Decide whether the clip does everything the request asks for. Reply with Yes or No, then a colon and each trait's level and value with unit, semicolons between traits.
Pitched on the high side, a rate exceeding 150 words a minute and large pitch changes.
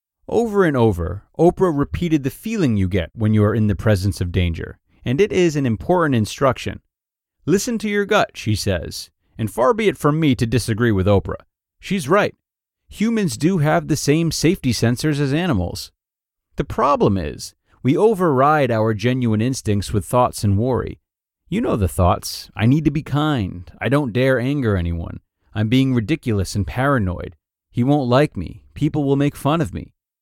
No: low, 120 Hz; average, 180 wpm; wide, 7.2 semitones